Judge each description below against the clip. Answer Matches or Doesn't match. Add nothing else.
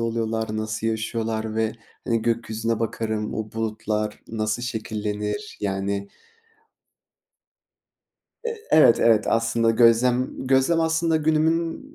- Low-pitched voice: Matches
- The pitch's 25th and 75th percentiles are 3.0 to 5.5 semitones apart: Doesn't match